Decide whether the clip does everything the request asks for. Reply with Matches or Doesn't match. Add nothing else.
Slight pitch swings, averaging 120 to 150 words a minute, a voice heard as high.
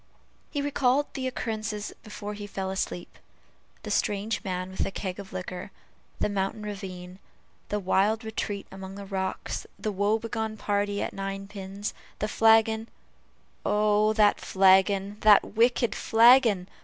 Matches